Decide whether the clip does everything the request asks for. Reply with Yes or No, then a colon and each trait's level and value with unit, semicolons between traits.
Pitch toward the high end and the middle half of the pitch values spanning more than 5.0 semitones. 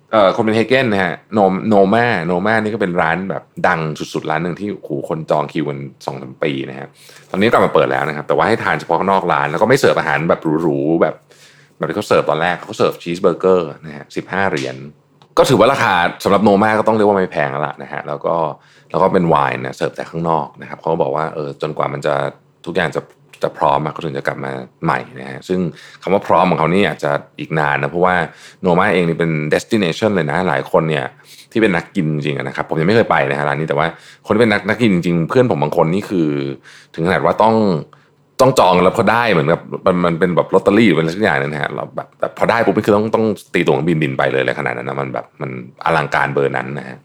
No: very low, 80 Hz; wide, 5.5 semitones